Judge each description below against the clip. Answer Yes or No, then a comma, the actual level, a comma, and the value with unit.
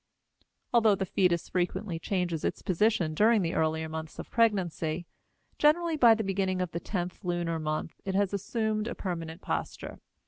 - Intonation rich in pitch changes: No, average, 4.3 semitones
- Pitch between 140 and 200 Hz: Yes, medium, 185 Hz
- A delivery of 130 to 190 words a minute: Yes, average, 165 wpm